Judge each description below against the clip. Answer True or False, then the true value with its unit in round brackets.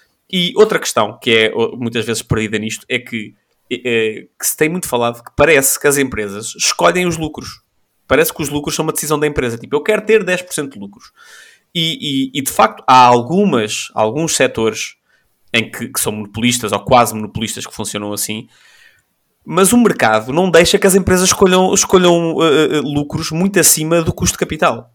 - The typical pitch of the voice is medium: True (145 Hz)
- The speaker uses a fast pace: True (190 wpm)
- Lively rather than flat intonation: True (7.4 semitones)